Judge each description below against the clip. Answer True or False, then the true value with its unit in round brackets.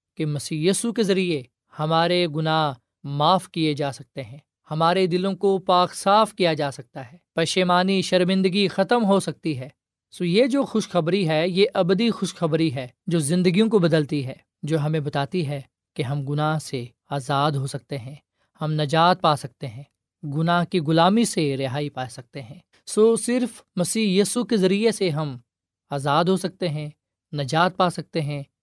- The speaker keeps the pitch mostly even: False (4.7 semitones)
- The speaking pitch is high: False (160 Hz)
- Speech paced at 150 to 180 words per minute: True (170 wpm)